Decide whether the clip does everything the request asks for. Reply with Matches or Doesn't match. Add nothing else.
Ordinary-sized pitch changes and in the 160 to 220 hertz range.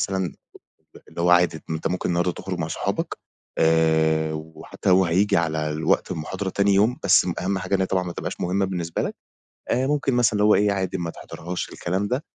Doesn't match